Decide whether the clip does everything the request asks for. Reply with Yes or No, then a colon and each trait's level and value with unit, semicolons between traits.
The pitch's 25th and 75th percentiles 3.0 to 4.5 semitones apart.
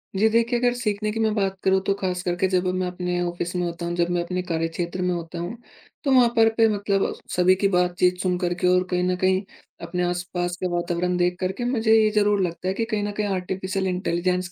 No: narrow, 2.4 semitones